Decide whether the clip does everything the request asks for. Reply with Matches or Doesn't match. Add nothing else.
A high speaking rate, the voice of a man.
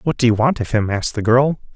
Matches